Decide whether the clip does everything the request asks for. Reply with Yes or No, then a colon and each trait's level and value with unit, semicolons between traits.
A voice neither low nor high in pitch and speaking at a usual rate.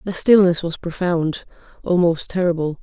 No: medium, 175 Hz; slow, 125 wpm